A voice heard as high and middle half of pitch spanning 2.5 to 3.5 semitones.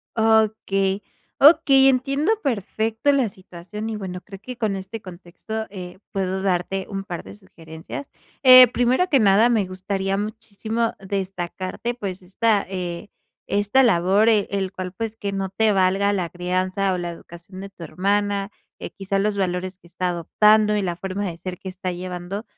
Yes: high, 195 Hz; average, 2.9 semitones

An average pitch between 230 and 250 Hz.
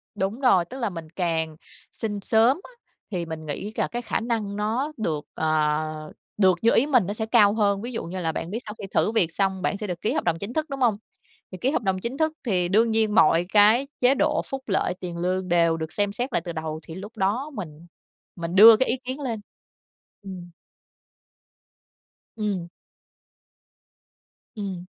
No: high, 205 Hz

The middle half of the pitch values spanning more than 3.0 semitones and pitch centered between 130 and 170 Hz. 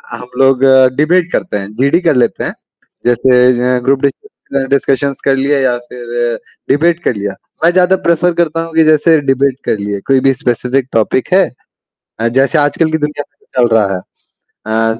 Yes: average, 4.3 semitones; low, 135 Hz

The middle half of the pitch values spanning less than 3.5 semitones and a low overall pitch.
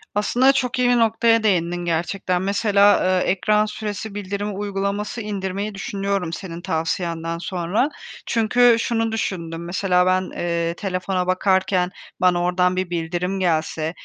No: average, 2.9 semitones; high, 190 Hz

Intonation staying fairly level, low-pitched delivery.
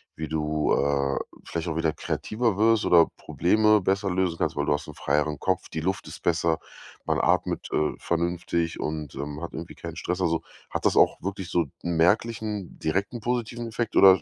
No: average, 4.0 semitones; very low, 85 Hz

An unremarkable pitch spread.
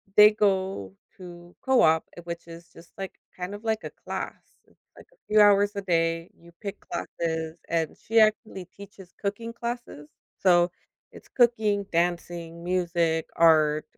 Yes: average, 3.7 semitones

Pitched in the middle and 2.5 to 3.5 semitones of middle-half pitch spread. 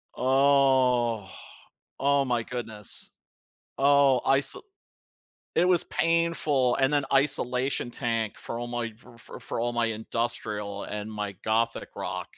No: low, 125 Hz; average, 3.2 semitones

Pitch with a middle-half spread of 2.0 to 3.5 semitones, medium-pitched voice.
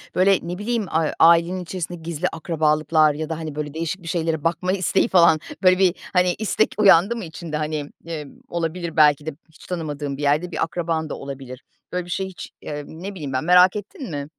Yes: average, 3.0 semitones; medium, 165 Hz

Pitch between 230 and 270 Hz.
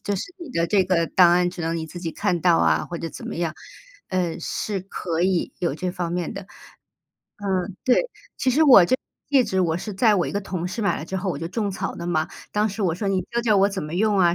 No: medium, 185 Hz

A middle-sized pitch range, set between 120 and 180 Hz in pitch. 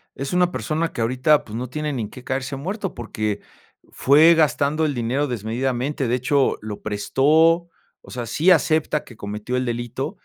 Yes: average, 4.3 semitones; low, 135 Hz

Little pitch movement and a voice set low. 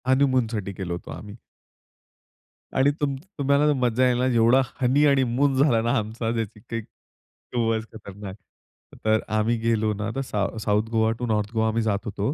No: average, 3.1 semitones; low, 115 Hz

